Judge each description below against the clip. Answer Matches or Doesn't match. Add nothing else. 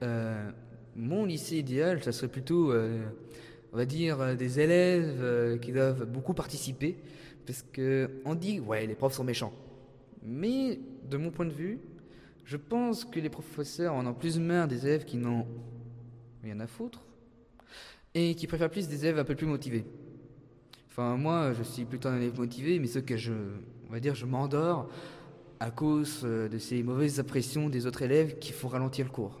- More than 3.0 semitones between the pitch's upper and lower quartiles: Matches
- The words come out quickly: Doesn't match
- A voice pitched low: Matches